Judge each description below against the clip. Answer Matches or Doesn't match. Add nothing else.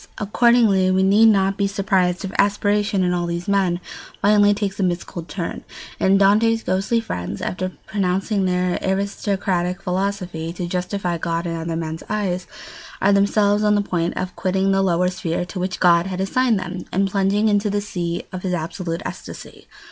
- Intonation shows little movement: Matches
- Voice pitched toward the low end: Doesn't match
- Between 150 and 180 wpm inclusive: Matches